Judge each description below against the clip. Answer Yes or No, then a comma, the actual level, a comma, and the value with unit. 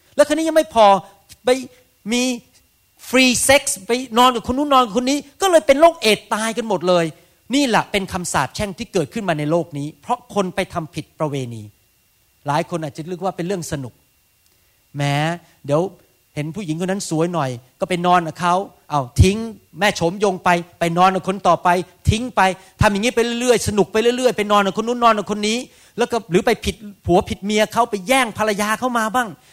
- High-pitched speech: Yes, high, 195 Hz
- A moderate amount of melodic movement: No, wide, 5.7 semitones